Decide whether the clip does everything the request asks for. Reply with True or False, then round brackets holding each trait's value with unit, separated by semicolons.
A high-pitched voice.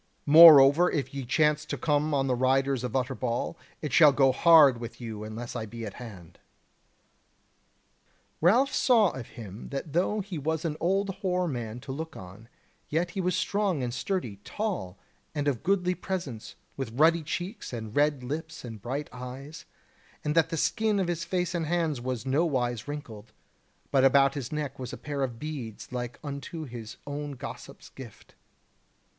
False (145 Hz)